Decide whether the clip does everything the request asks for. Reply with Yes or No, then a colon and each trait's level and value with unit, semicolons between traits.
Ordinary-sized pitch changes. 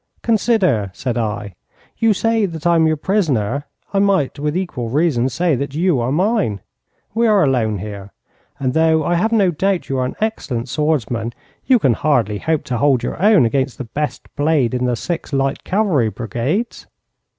No: wide, 7.2 semitones